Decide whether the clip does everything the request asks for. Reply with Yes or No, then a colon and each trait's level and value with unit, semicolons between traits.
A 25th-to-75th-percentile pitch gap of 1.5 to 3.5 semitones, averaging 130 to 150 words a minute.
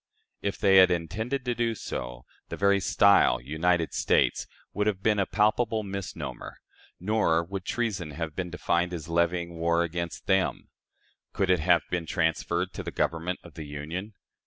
No: average, 3.2 semitones; average, 165 wpm